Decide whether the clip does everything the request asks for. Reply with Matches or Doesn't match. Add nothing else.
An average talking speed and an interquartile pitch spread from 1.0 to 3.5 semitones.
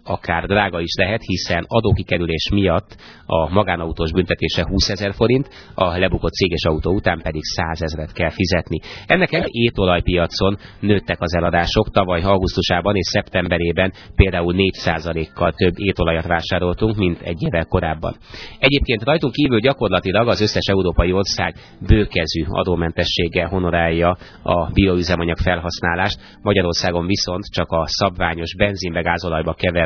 Matches